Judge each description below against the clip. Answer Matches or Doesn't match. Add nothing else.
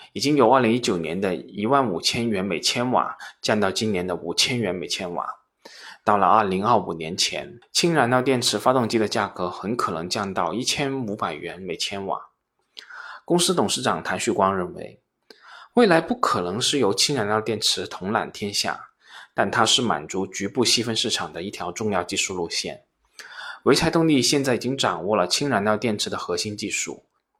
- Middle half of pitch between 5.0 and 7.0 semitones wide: Matches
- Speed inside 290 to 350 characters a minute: Doesn't match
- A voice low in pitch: Matches